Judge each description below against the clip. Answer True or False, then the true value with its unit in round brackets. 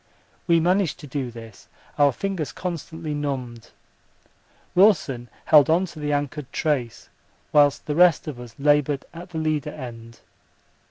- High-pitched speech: False (145 Hz)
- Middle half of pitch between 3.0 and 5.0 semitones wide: True (4.0 semitones)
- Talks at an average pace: True (145 wpm)